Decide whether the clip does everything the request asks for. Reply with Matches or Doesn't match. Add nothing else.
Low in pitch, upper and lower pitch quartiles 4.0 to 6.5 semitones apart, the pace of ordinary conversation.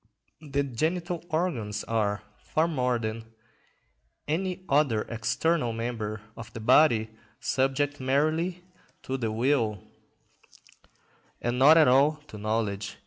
Doesn't match